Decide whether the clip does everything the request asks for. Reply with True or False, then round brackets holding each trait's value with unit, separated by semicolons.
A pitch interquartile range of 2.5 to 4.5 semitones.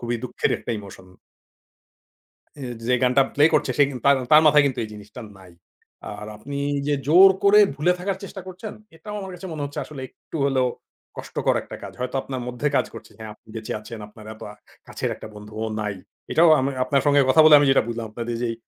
False (5.2 semitones)